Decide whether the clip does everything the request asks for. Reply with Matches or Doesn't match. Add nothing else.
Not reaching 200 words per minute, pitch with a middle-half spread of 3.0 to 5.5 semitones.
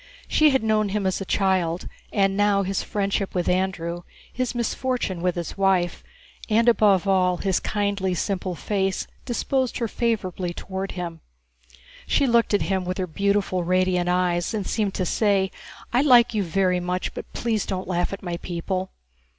Doesn't match